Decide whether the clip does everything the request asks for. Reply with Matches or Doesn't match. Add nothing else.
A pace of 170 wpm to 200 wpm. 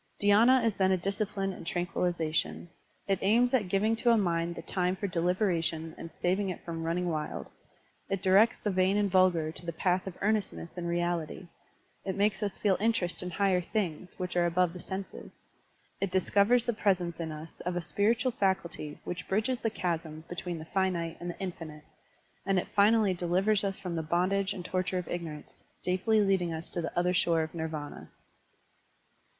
Matches